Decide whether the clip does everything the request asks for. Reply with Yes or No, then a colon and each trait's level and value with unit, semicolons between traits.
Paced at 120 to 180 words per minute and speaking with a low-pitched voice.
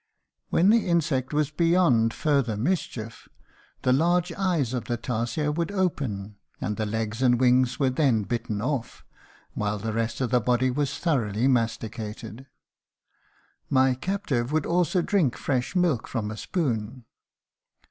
Yes: average, 145 wpm; low, 130 Hz